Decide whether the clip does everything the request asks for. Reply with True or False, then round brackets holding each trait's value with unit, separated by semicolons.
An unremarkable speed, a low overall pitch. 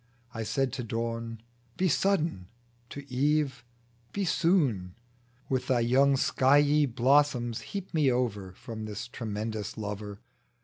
False (130 wpm; 125 Hz)